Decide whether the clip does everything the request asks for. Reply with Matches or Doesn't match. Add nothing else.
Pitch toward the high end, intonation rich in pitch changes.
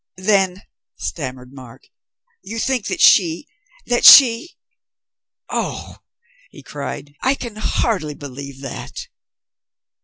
Doesn't match